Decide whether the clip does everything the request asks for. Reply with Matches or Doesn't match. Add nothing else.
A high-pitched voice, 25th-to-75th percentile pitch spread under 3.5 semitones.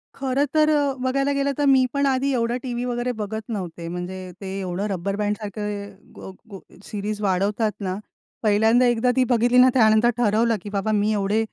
Doesn't match